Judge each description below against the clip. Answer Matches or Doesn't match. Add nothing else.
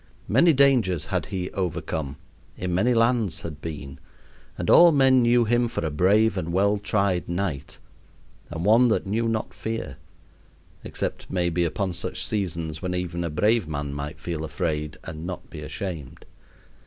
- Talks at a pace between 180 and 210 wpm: Doesn't match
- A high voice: Doesn't match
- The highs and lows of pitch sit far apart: Matches